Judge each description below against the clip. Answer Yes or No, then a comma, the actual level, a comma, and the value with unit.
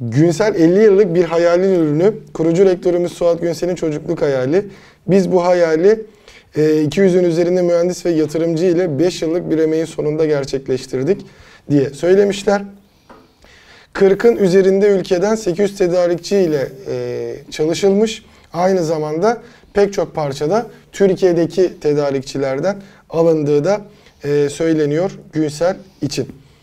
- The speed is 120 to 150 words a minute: No, average, 110 wpm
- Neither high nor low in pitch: Yes, medium, 175 Hz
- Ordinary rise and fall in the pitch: Yes, average, 4.0 semitones